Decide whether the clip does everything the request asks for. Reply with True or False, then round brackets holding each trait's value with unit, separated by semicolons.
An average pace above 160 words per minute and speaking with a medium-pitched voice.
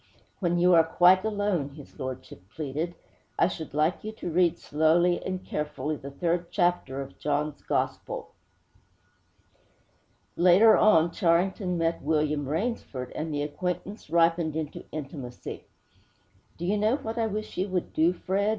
False (145 wpm; 170 Hz)